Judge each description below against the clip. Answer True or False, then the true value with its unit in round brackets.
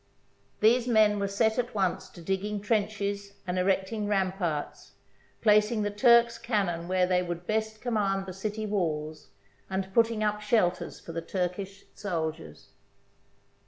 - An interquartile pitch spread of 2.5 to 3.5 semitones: True (2.9 semitones)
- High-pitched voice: True (200 Hz)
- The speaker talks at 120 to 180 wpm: True (145 wpm)